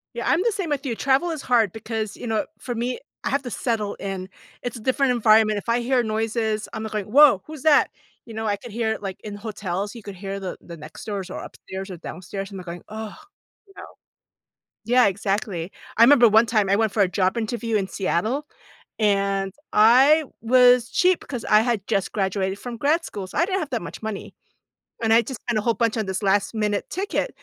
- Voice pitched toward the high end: Yes, high, 220 Hz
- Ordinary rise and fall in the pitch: Yes, average, 3.7 semitones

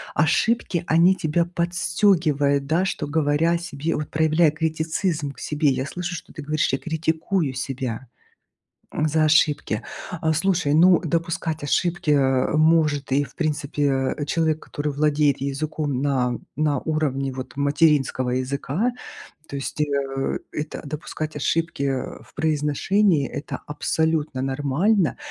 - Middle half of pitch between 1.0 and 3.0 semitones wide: Yes, average, 2.7 semitones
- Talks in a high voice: No, medium, 150 Hz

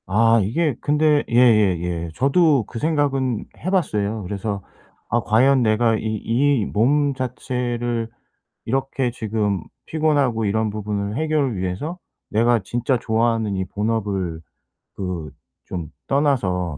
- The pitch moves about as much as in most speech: Yes, average, 4.9 semitones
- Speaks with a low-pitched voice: Yes, low, 115 Hz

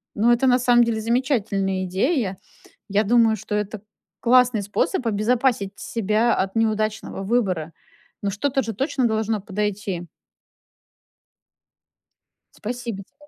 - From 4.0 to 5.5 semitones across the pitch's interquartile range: No, average, 3.3 semitones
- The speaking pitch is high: Yes, high, 220 Hz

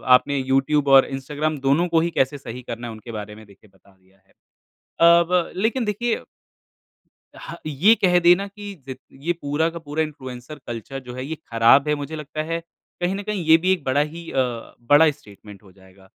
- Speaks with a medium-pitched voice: Yes, medium, 145 Hz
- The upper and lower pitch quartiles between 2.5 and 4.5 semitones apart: No, wide, 5.6 semitones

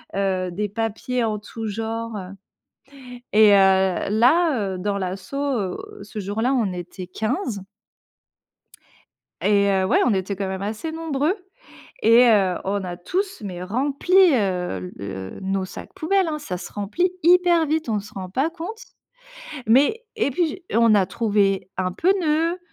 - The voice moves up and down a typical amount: No, wide, 7.2 semitones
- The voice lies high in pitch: Yes, high, 215 Hz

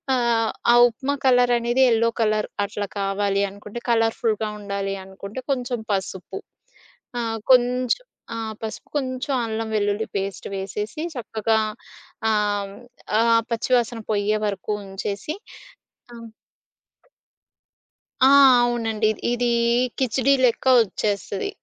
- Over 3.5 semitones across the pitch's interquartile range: No, average, 3.0 semitones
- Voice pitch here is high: Yes, high, 220 Hz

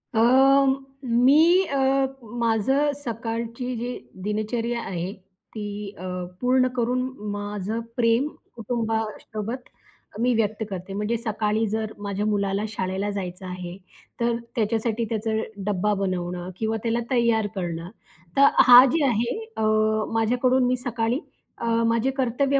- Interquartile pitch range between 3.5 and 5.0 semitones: No, average, 3.1 semitones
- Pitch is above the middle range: Yes, high, 225 Hz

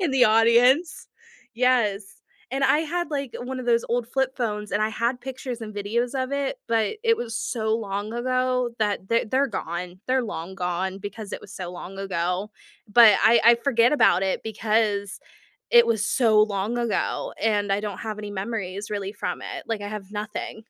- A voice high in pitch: Yes, high, 225 Hz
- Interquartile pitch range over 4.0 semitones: No, average, 3.4 semitones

